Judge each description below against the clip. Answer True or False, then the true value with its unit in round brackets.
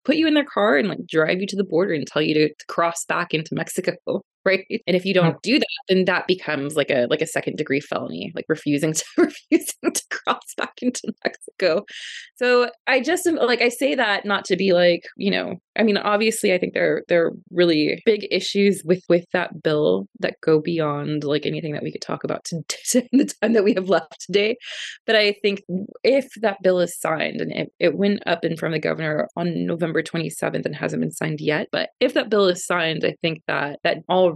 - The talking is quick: True (230 wpm)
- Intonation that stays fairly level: False (5.5 semitones)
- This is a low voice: False (185 Hz)